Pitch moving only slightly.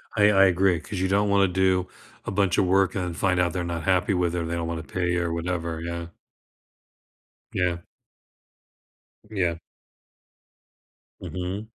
Yes: narrow, 2.1 semitones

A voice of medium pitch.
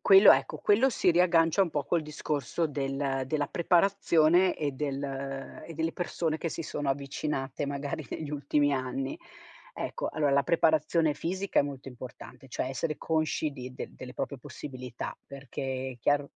Yes: medium, 145 Hz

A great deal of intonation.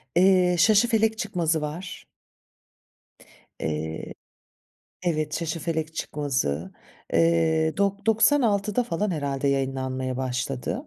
Yes: wide, 6.6 semitones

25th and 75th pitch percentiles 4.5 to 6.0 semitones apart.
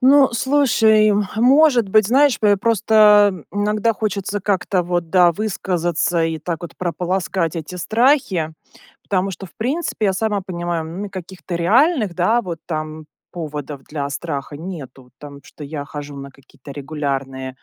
Yes: wide, 5.5 semitones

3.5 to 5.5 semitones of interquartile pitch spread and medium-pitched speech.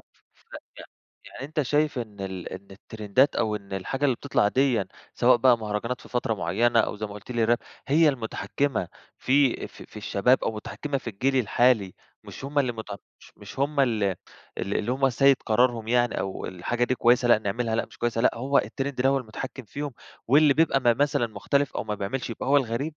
No: average, 4.1 semitones; low, 120 Hz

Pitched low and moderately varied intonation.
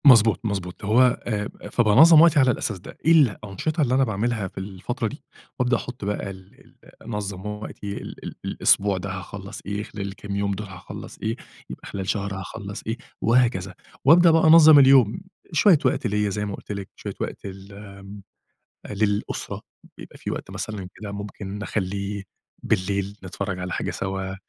Yes: low, 105 Hz; average, 3.4 semitones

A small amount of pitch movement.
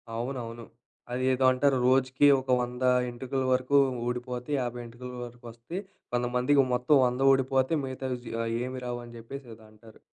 Yes: narrow, 1.4 semitones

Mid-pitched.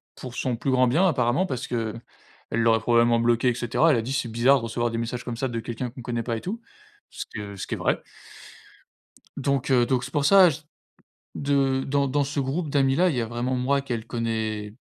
No: low, 125 Hz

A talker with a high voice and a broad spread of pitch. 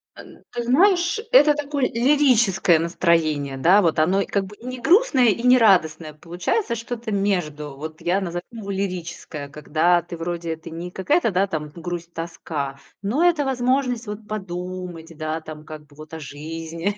No: medium, 180 Hz; wide, 6.4 semitones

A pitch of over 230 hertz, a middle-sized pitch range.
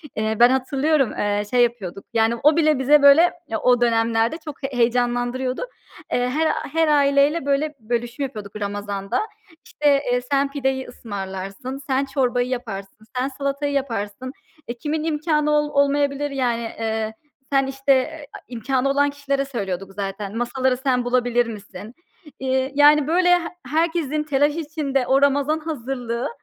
Yes: very high, 265 Hz; average, 3.4 semitones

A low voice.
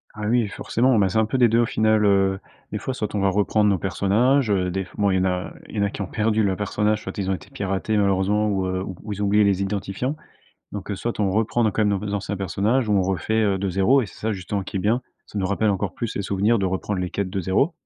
Yes: low, 100 Hz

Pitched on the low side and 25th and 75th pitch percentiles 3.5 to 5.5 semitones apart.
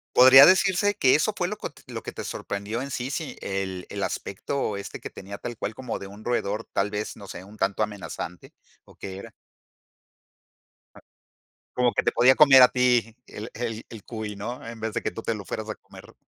Yes: low, 110 Hz; average, 4.1 semitones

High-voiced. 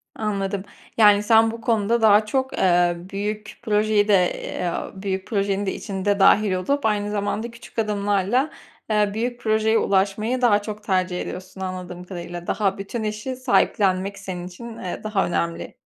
Yes: high, 205 Hz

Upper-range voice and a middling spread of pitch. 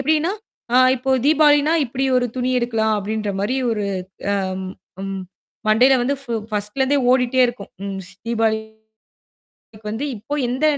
Yes: high, 240 Hz; average, 3.7 semitones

